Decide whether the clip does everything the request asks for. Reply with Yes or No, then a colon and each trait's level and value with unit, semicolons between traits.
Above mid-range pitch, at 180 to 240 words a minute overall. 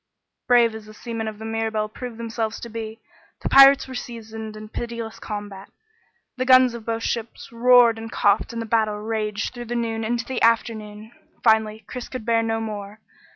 Yes: high, 225 Hz; average, 190 wpm